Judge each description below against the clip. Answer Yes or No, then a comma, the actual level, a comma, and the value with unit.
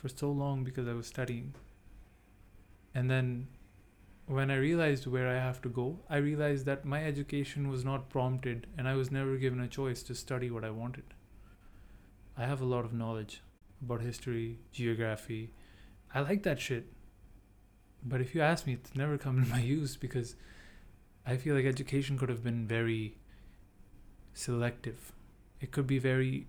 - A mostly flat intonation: No, average, 4.6 semitones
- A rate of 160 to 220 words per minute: Yes, average, 170 wpm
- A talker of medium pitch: No, low, 125 Hz